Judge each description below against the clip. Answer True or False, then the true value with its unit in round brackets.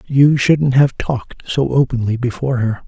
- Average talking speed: True (165 wpm)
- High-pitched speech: False (130 Hz)